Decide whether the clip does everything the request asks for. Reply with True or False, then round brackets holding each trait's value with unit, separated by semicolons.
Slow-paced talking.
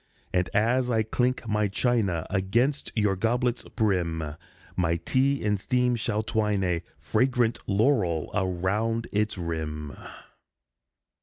True (120 wpm)